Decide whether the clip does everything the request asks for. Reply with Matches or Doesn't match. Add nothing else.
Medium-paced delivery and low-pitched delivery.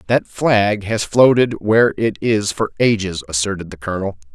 Matches